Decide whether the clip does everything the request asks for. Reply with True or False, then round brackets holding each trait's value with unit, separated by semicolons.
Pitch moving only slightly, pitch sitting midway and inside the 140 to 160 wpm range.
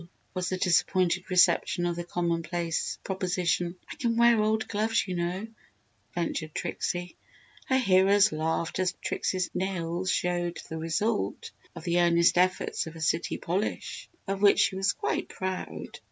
True (2.1 semitones; 180 Hz; 155 wpm)